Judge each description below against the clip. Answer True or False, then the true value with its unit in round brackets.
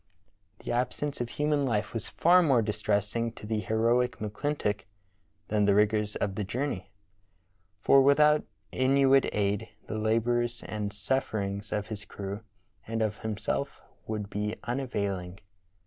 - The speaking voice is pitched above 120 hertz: False (110 Hz)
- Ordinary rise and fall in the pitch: True (3.4 semitones)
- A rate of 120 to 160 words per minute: True (140 wpm)